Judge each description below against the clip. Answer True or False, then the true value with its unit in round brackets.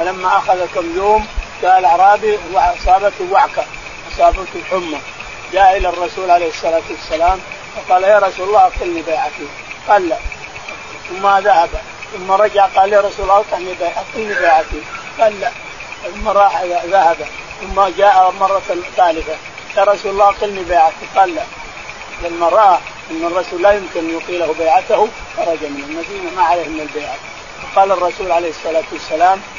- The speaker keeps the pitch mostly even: False (3.4 semitones)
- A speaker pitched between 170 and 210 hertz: True (190 Hz)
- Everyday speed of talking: False (140 wpm)